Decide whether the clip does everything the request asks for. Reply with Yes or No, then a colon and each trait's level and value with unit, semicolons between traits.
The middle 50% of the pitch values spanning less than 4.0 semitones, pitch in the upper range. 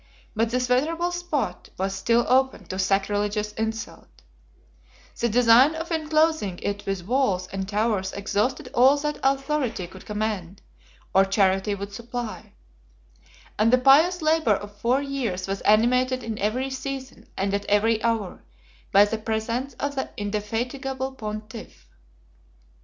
No: average, 4.5 semitones; high, 225 Hz